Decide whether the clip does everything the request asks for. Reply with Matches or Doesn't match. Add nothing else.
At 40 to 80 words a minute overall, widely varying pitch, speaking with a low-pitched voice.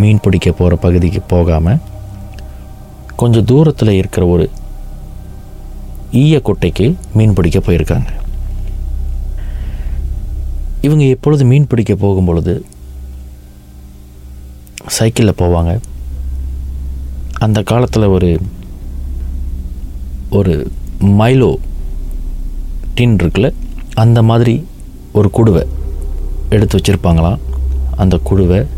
Matches